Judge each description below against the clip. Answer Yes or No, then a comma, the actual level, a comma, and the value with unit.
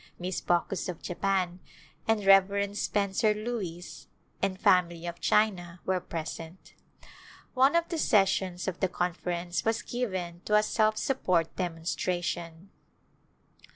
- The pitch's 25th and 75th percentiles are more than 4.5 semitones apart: No, average, 3.2 semitones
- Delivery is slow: Yes, slow, 120 wpm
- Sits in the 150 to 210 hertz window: Yes, medium, 185 Hz